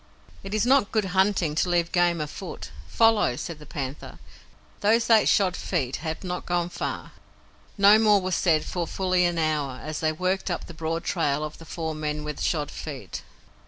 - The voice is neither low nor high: Yes, medium, 170 Hz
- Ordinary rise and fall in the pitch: Yes, average, 3.7 semitones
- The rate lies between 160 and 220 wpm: Yes, average, 190 wpm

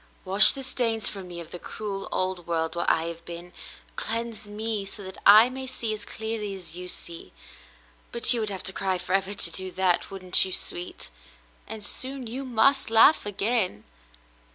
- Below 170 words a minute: No, average, 185 wpm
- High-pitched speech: Yes, high, 200 Hz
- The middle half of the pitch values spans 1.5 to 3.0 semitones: No, average, 3.7 semitones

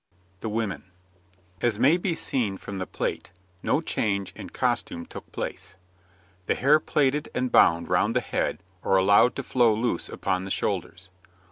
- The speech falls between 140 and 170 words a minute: Yes, average, 160 wpm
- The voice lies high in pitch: No, low, 105 Hz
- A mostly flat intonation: No, average, 5.0 semitones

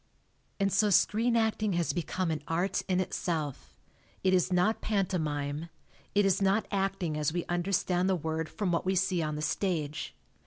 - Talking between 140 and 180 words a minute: Yes, average, 170 wpm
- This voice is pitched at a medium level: Yes, medium, 180 Hz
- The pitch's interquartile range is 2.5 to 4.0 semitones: Yes, average, 3.5 semitones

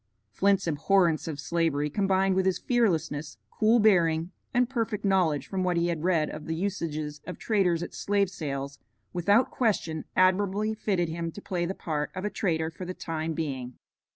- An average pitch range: Yes, average, 3.7 semitones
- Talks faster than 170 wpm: Yes, average, 180 wpm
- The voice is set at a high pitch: No, medium, 175 Hz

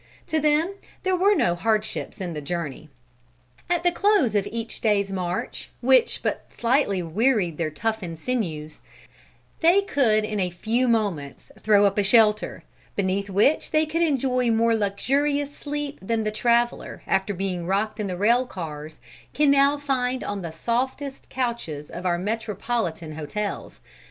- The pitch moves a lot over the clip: Yes, wide, 6.0 semitones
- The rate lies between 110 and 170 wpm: Yes, average, 155 wpm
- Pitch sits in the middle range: No, high, 215 Hz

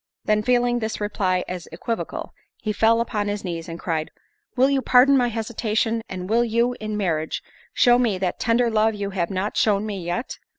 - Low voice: No, high, 215 Hz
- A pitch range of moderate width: Yes, average, 3.9 semitones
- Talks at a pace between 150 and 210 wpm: Yes, average, 195 wpm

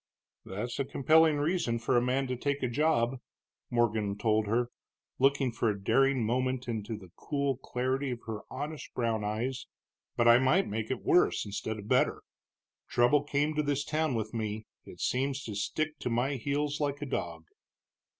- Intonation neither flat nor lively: Yes, average, 4.1 semitones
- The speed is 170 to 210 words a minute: Yes, average, 180 wpm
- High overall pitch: No, low, 125 Hz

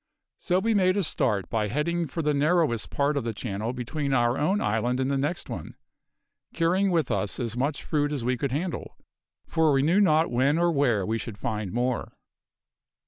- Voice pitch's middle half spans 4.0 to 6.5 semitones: Yes, wide, 5.6 semitones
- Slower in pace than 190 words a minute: No, average, 195 wpm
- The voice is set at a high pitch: No, medium, 140 Hz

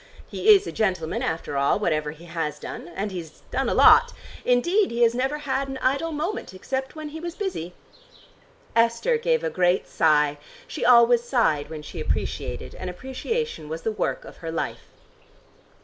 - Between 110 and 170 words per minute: No, average, 180 wpm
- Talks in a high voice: Yes, high, 235 Hz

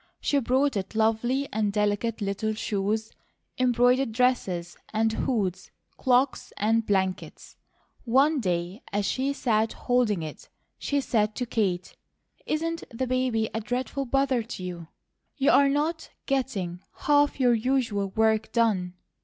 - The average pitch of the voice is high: Yes, high, 225 Hz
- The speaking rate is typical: No, slow, 130 wpm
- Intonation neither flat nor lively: Yes, average, 4.2 semitones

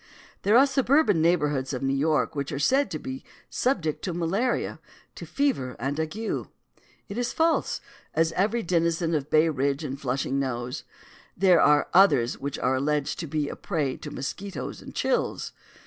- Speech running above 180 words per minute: No, average, 170 wpm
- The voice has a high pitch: No, medium, 160 Hz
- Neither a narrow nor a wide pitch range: No, wide, 6.4 semitones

